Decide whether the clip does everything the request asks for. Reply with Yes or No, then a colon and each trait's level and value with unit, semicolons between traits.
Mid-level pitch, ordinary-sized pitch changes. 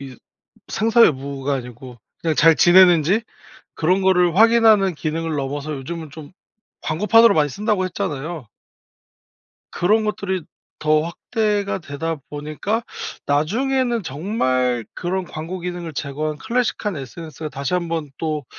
Yes: medium, 165 Hz; average, 5.0 semitones